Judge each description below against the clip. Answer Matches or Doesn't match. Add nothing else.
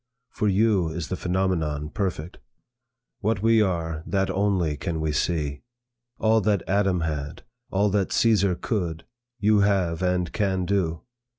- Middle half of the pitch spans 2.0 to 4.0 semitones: Matches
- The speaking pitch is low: Matches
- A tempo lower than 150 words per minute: Matches